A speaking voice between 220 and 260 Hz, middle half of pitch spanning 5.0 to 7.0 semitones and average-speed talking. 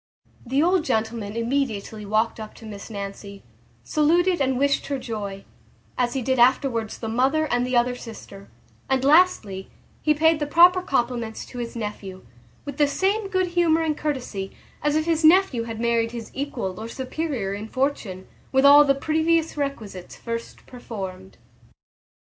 Yes: very high, 250 Hz; average, 5.3 semitones; average, 160 wpm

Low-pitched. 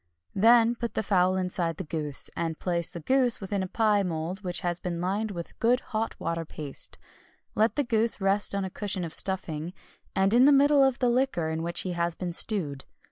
No: high, 190 Hz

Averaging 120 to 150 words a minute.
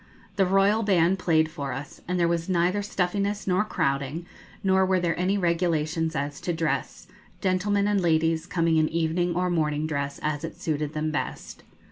No: average, 175 wpm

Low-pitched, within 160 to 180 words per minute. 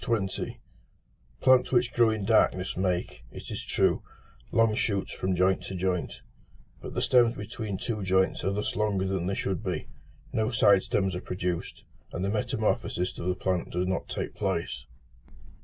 Yes: very low, 95 Hz; average, 165 wpm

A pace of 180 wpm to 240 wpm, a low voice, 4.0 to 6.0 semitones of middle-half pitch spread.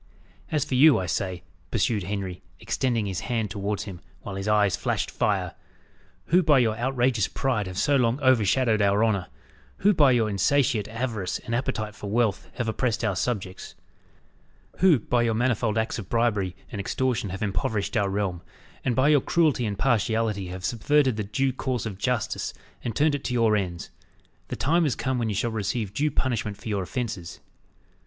Yes: average, 185 wpm; low, 115 Hz; average, 4.3 semitones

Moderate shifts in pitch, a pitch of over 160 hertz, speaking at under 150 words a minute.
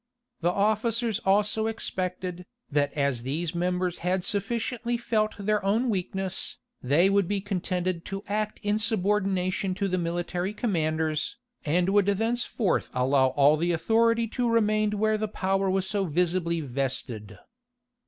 Yes: average, 3.8 semitones; high, 190 Hz; average, 140 wpm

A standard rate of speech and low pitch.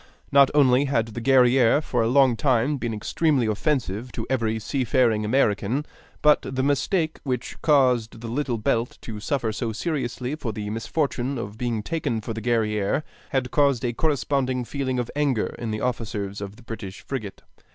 Yes: average, 170 wpm; low, 125 Hz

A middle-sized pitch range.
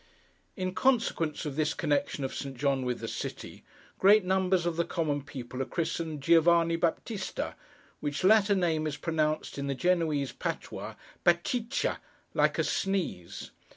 Yes: average, 4.2 semitones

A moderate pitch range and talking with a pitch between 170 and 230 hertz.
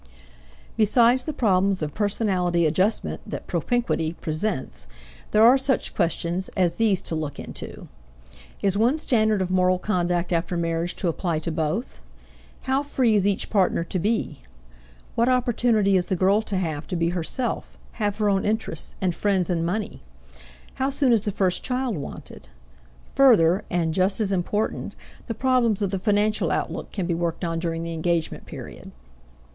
Yes: average, 4.4 semitones; high, 190 Hz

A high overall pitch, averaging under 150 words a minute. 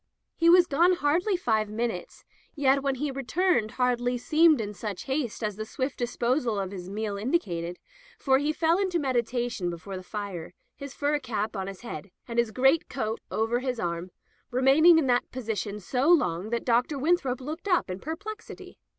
No: very high, 250 Hz; average, 180 wpm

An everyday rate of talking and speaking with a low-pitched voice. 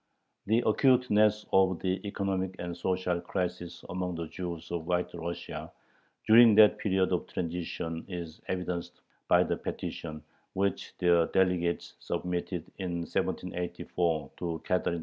No: slow, 130 wpm; very low, 90 Hz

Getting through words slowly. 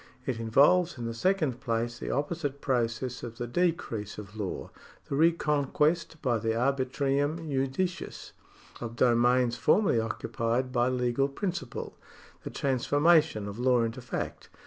No: average, 145 wpm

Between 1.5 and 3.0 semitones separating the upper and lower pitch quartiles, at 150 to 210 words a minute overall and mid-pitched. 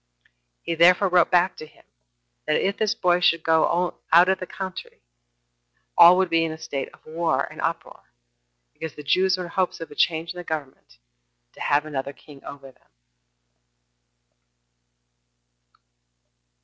Yes: average, 2.7 semitones; average, 165 wpm; medium, 165 Hz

